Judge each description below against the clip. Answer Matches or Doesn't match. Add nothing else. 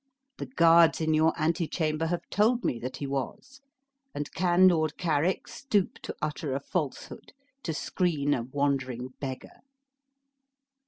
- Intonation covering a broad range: Doesn't match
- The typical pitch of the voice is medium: Matches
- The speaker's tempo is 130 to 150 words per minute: Matches